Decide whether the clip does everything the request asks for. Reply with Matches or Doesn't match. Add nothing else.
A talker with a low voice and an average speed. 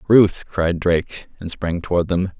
Matches